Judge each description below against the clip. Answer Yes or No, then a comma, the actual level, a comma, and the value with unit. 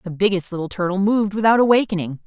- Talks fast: No, average, 185 wpm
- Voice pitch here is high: Yes, high, 195 Hz